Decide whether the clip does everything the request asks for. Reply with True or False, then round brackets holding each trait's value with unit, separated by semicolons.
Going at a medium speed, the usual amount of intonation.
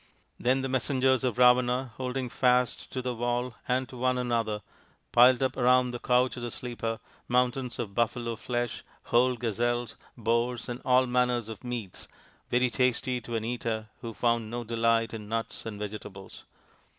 False (165 wpm; 1.6 semitones)